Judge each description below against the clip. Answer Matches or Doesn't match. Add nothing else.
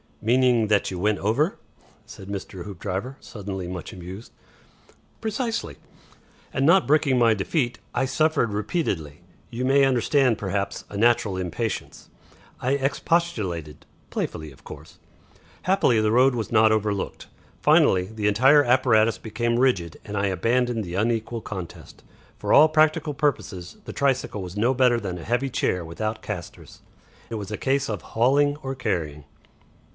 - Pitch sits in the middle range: Doesn't match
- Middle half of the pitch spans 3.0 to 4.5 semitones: Doesn't match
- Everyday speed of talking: Matches